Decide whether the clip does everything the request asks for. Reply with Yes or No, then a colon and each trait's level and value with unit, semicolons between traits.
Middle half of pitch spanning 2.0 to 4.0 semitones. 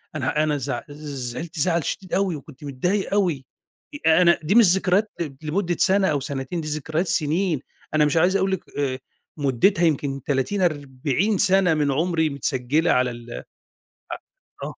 No: average, 4.6 semitones